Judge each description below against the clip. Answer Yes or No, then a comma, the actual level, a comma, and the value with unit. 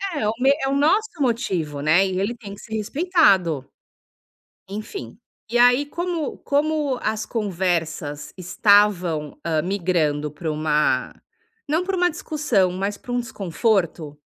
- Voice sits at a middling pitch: No, high, 200 Hz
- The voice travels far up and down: Yes, wide, 8.0 semitones